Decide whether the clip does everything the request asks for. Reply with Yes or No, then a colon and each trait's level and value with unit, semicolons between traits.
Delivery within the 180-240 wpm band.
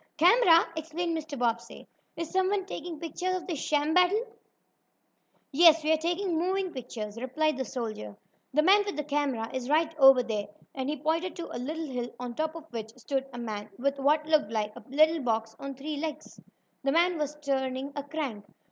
Yes: average, 190 wpm